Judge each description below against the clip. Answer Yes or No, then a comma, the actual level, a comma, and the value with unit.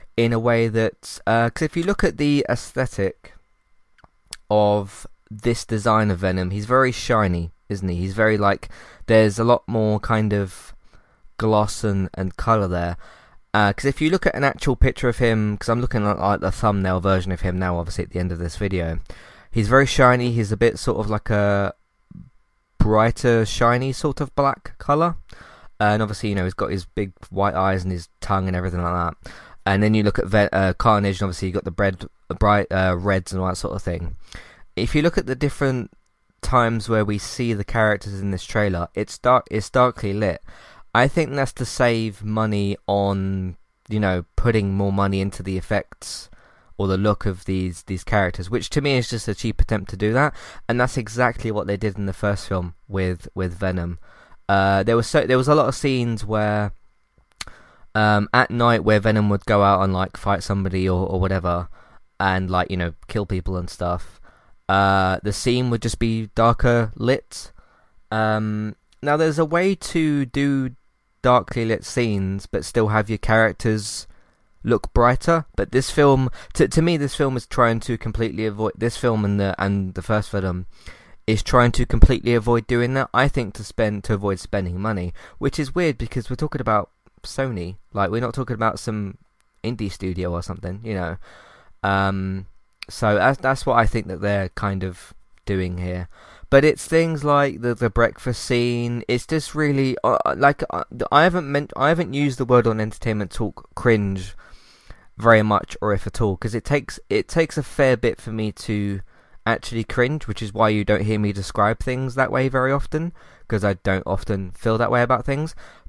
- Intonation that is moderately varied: Yes, average, 4.0 semitones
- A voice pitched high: No, low, 110 Hz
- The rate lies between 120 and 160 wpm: No, average, 200 wpm